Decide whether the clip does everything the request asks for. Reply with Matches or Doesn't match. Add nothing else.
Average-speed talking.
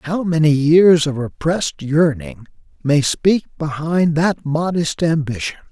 Doesn't match